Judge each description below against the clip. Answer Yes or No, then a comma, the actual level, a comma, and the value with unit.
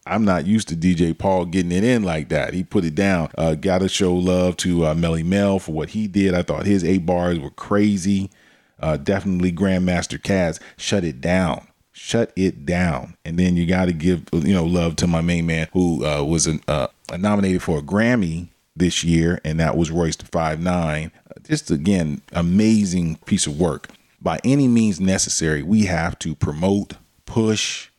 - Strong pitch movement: No, average, 3.0 semitones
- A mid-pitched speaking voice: No, very low, 90 Hz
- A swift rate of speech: No, average, 190 wpm